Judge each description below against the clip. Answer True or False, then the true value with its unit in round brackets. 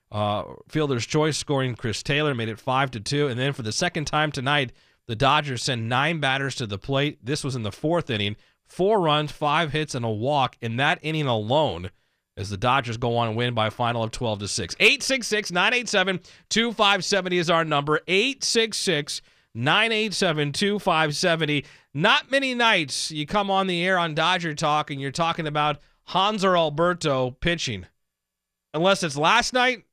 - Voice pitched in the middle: True (150 Hz)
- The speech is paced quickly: False (180 wpm)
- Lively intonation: True (6.1 semitones)